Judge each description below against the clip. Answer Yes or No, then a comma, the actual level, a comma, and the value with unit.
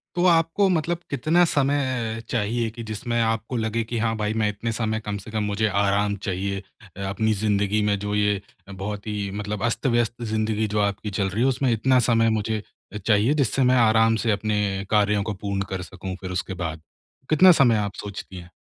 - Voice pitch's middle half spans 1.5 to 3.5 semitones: Yes, narrow, 2.5 semitones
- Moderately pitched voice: No, low, 110 Hz